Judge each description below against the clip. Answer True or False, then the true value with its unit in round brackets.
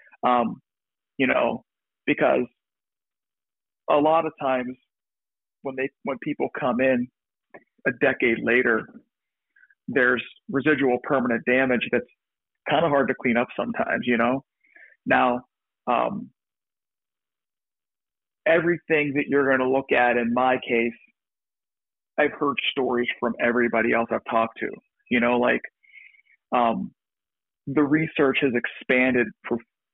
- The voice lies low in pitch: True (130 Hz)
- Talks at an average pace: False (120 wpm)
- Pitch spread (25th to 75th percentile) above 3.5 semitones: False (3.1 semitones)